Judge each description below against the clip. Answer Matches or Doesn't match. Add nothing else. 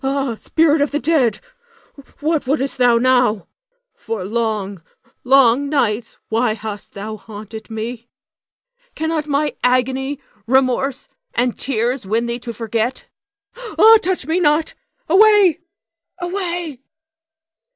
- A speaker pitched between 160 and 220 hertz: Doesn't match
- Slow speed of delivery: Matches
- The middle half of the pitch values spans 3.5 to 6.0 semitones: Matches